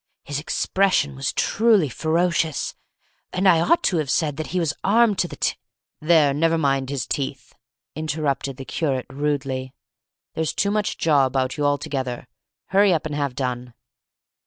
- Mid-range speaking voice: Yes, medium, 150 Hz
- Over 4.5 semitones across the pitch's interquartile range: No, average, 3.8 semitones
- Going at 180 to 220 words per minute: No, average, 165 wpm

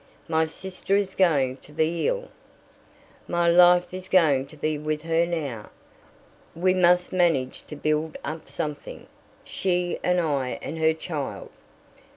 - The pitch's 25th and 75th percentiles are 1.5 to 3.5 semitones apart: Yes, average, 2.8 semitones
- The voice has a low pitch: No, medium, 160 Hz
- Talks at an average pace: Yes, average, 145 wpm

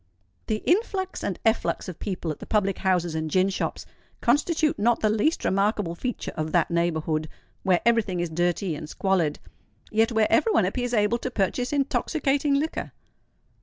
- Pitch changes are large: Yes, wide, 6.0 semitones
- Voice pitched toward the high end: Yes, high, 205 Hz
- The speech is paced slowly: No, average, 170 wpm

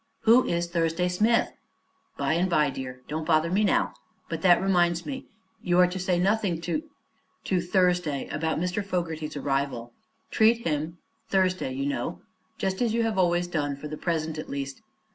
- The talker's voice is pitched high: No, medium, 175 Hz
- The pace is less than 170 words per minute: No, average, 175 wpm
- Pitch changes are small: No, average, 3.4 semitones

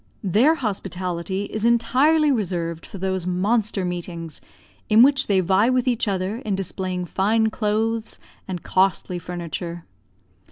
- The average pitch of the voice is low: No, high, 195 Hz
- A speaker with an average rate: No, slow, 130 wpm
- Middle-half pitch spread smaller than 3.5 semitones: No, average, 4.0 semitones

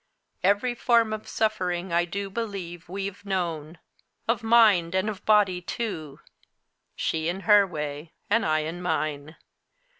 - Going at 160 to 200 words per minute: No, average, 140 wpm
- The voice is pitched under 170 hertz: No, medium, 185 Hz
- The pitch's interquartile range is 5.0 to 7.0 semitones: No, average, 4.2 semitones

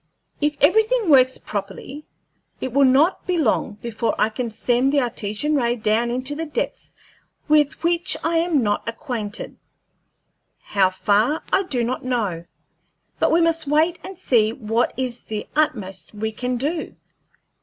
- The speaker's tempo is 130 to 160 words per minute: Yes, average, 150 wpm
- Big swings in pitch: Yes, wide, 5.7 semitones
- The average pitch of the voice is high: Yes, very high, 255 Hz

